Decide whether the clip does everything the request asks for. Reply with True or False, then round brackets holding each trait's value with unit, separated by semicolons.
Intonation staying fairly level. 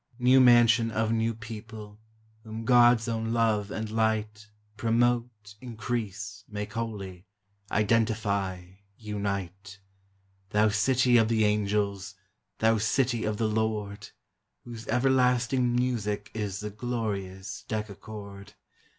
True (1.9 semitones)